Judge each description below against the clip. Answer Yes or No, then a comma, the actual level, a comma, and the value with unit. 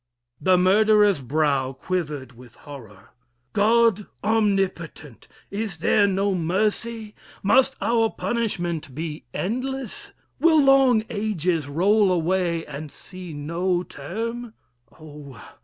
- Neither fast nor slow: No, slow, 105 wpm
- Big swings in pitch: Yes, wide, 5.9 semitones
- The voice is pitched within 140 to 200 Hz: Yes, medium, 185 Hz